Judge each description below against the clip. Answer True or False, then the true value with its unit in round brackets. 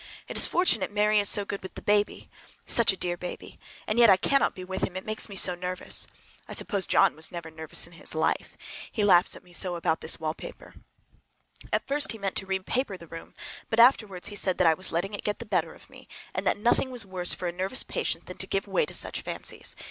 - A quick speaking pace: True (245 wpm)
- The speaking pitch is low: False (190 Hz)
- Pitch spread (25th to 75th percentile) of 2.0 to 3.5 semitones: True (3.2 semitones)